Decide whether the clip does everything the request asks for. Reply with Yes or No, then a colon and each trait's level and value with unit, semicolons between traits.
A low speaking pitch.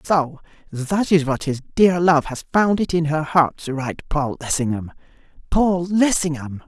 No: medium, 155 Hz